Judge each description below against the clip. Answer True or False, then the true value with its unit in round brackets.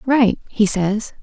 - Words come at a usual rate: True (145 wpm)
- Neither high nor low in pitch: False (220 Hz)